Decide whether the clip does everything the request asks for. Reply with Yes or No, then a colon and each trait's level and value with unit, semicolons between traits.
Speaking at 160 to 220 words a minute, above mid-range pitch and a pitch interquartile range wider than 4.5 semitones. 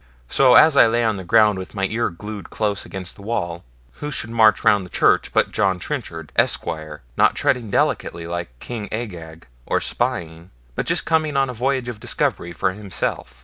No: average, 190 wpm; low, 105 Hz; average, 5.3 semitones